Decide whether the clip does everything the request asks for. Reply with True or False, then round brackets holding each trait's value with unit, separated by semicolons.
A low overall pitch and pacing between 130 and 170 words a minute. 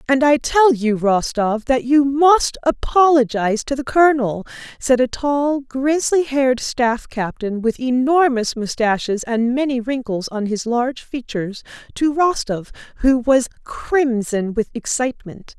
False (255 Hz; 140 wpm)